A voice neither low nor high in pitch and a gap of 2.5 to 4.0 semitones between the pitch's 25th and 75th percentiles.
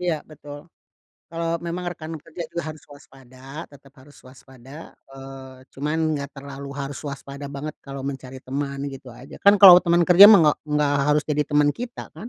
Yes: medium, 145 Hz; average, 2.9 semitones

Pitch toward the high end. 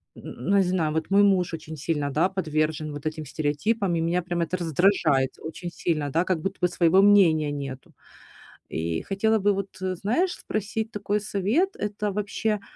No: medium, 180 Hz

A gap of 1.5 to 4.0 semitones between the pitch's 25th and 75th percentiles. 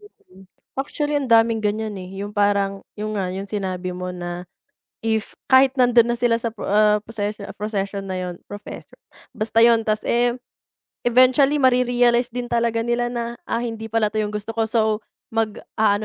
Yes: average, 2.7 semitones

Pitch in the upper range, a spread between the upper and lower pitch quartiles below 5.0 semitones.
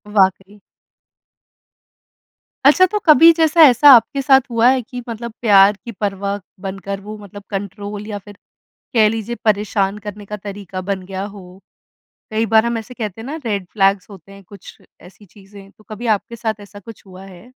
Yes: high, 205 Hz; average, 2.8 semitones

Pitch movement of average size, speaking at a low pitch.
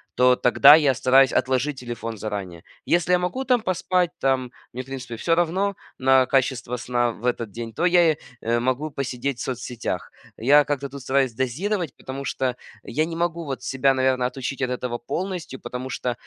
Yes: average, 3.8 semitones; low, 130 Hz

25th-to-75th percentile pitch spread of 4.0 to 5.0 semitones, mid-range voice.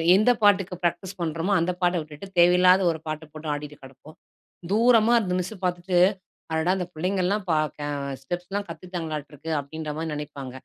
No: average, 3.3 semitones; medium, 175 Hz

